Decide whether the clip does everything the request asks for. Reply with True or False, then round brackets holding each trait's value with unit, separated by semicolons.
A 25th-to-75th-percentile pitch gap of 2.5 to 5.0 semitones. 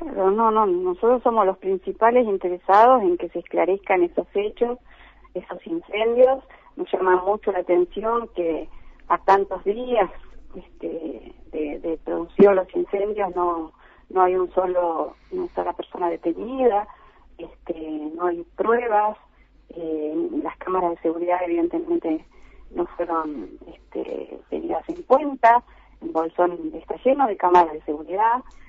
False (5.6 semitones)